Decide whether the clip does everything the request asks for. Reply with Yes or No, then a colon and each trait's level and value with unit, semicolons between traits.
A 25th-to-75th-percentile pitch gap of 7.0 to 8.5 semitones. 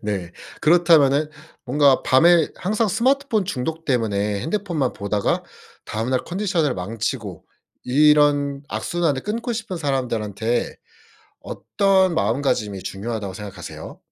Yes: wide, 7.9 semitones